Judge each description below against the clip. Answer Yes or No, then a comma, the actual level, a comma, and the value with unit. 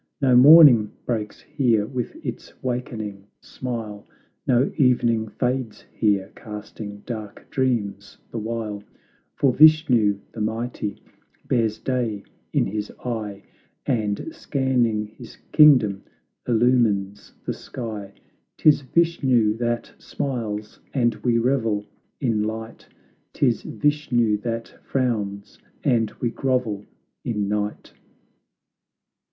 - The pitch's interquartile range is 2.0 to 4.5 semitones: Yes, average, 3.2 semitones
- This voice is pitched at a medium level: No, low, 115 Hz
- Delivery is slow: Yes, slow, 105 wpm